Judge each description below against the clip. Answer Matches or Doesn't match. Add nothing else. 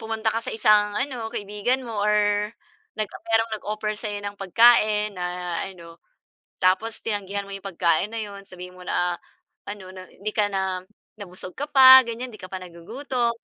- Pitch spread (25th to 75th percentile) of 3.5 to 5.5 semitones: Doesn't match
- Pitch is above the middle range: Matches